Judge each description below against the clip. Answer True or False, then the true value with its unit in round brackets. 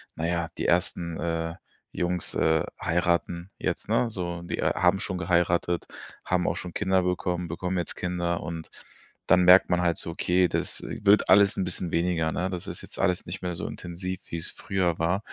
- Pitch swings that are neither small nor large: False (1.2 semitones)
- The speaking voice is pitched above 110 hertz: False (90 Hz)